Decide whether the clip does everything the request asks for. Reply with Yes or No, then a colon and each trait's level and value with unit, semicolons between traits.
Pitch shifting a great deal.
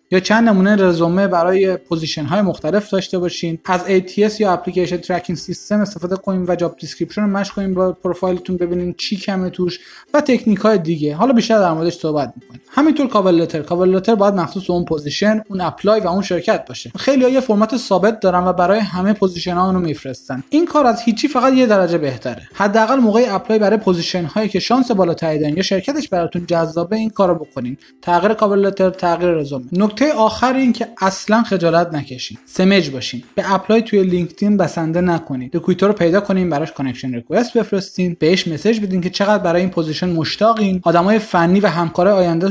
No: average, 3.6 semitones